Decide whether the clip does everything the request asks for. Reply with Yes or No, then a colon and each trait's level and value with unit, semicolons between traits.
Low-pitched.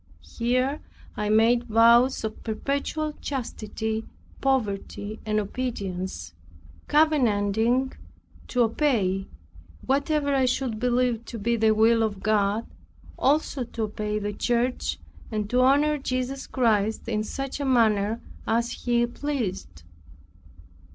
No: high, 235 Hz